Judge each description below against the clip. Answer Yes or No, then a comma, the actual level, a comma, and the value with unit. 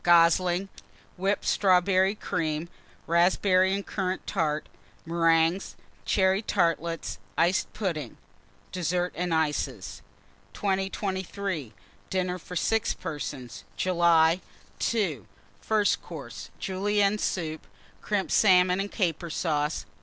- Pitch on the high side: No, medium, 180 Hz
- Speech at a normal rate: No, slow, 95 wpm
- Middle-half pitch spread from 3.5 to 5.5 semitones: No, average, 2.9 semitones